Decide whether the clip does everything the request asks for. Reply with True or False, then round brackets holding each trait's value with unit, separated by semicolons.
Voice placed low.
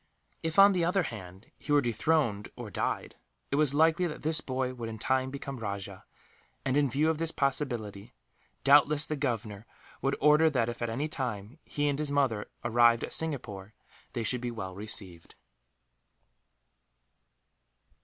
True (130 Hz)